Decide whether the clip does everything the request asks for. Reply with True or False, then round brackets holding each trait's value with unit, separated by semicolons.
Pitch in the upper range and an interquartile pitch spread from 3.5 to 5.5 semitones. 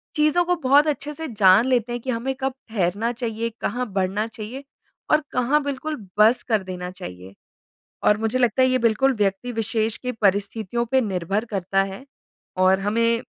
True (230 Hz; 4.3 semitones)